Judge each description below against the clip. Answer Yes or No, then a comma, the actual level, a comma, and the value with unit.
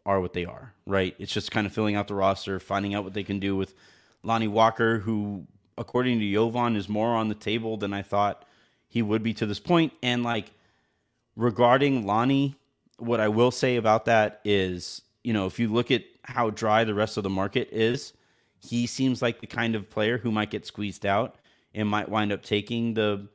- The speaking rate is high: Yes, fast, 215 wpm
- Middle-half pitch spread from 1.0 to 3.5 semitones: Yes, narrow, 2.5 semitones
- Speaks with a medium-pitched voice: No, low, 110 Hz